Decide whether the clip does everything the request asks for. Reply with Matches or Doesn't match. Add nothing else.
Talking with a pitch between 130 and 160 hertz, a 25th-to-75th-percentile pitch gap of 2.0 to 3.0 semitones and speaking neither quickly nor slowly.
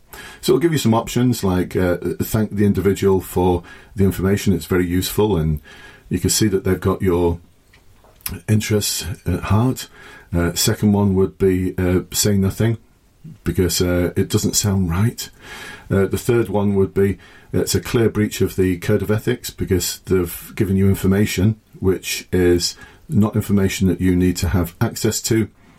Doesn't match